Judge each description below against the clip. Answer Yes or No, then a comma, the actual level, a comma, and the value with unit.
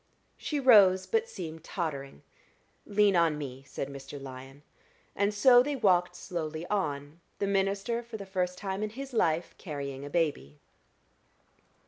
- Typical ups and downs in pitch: No, wide, 6.0 semitones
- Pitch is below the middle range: No, medium, 180 Hz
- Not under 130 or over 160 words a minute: Yes, average, 145 wpm